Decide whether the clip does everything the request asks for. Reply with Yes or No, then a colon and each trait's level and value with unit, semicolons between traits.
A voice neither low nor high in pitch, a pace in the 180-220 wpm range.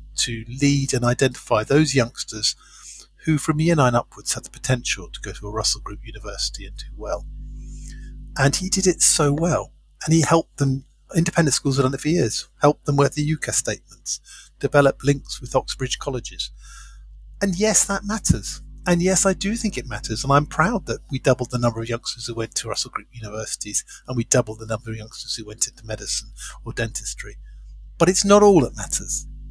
No: low, 130 Hz; average, 195 wpm